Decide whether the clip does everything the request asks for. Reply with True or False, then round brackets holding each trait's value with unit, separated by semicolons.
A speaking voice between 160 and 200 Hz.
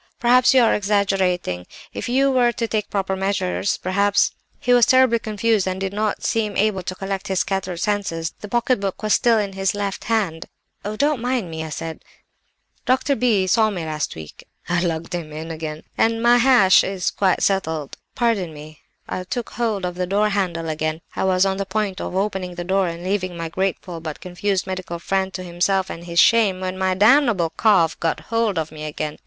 True (190 Hz)